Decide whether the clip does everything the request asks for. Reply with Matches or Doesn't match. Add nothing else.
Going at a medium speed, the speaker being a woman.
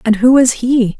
Doesn't match